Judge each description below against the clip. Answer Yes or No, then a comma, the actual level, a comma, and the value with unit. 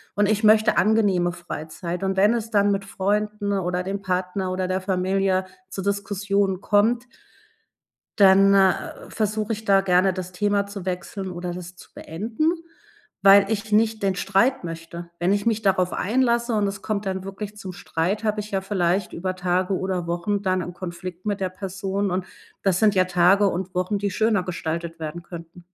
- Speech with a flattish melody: Yes, narrow, 2.2 semitones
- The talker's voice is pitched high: Yes, high, 195 Hz